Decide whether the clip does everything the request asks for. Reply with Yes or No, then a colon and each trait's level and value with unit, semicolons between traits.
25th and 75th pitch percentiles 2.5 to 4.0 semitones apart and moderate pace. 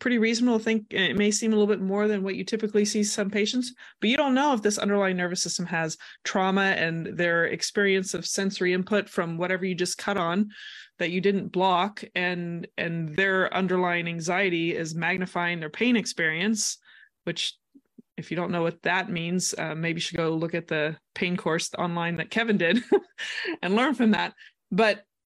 Yes: average, 3.5 semitones; average, 195 wpm